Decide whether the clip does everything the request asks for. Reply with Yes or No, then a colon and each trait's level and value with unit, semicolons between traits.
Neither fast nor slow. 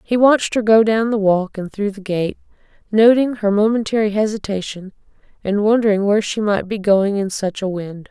Yes: average, 190 wpm